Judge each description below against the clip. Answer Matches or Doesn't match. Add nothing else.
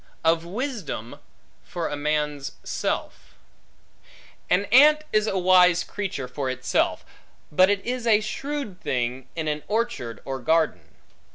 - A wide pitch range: Matches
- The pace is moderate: Doesn't match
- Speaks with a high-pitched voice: Doesn't match